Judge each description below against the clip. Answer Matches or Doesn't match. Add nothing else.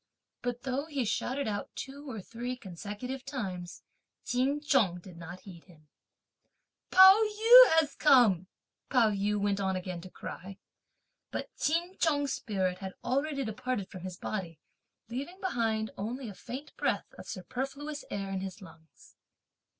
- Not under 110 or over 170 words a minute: Matches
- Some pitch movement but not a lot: Doesn't match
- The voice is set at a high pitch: Matches